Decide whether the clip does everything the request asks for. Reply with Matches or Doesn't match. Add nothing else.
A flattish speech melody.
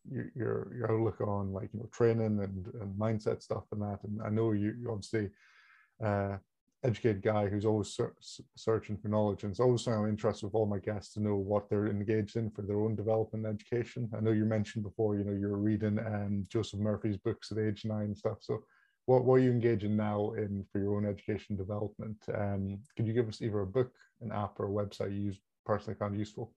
Matches